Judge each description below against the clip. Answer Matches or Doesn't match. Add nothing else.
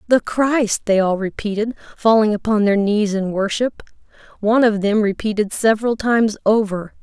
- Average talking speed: Matches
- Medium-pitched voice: Doesn't match